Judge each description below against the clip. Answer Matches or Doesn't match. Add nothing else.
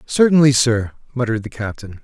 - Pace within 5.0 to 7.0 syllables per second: Matches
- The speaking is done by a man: Matches